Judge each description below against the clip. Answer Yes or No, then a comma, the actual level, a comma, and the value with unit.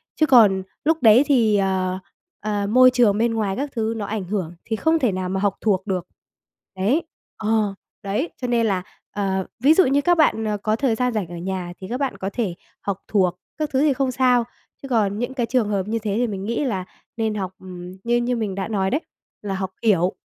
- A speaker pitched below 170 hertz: No, high, 215 Hz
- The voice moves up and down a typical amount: Yes, average, 4.3 semitones